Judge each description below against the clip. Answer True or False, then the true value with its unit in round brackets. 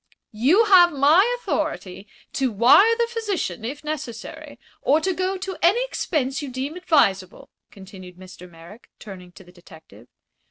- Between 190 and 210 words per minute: False (150 wpm)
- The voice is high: True (265 Hz)